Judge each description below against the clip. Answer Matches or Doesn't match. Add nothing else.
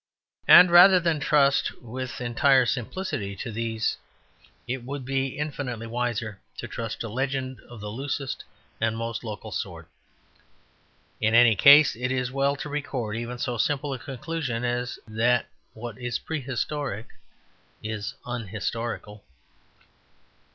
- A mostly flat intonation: Doesn't match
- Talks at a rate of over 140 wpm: Doesn't match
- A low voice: Matches